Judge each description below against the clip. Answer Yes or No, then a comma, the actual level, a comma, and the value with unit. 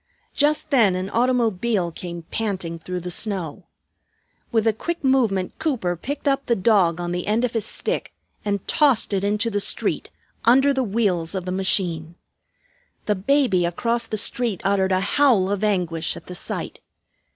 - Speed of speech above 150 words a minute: Yes, average, 170 wpm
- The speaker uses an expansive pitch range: No, average, 4.6 semitones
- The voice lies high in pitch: Yes, high, 205 Hz